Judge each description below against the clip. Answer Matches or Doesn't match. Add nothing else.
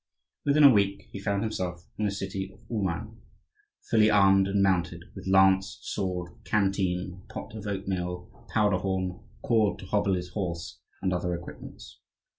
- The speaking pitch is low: Matches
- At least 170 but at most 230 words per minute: Doesn't match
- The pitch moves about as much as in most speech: Doesn't match